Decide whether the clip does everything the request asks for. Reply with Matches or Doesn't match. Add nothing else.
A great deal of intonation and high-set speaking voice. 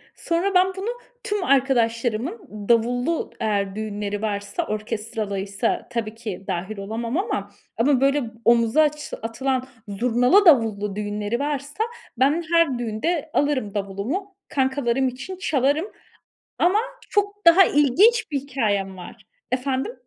Matches